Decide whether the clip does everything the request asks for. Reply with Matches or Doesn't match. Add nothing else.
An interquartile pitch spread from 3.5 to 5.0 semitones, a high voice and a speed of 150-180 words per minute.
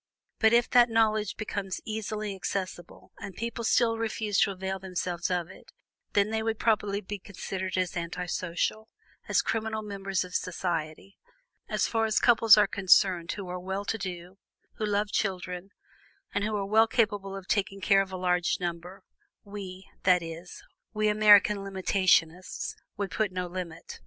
Doesn't match